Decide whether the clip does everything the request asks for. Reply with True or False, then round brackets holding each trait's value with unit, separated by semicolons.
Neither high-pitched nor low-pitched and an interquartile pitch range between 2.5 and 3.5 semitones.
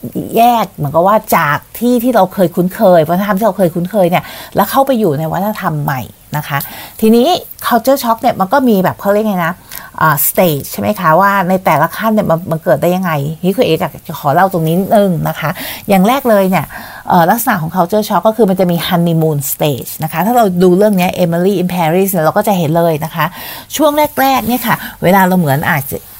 False (180 Hz; 4.8 semitones)